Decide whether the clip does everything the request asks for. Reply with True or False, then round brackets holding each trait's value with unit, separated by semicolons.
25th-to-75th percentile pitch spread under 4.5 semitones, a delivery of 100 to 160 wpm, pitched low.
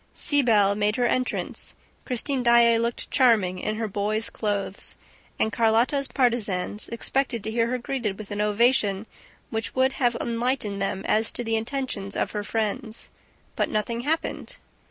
False (2.9 semitones; 155 wpm; 225 Hz)